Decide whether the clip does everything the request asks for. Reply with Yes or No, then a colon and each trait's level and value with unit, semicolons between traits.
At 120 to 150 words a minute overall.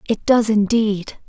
Yes: average, 140 wpm